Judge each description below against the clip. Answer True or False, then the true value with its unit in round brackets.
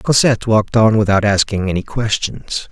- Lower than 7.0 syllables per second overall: True (5.4 syllables/s)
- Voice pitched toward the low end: True (105 Hz)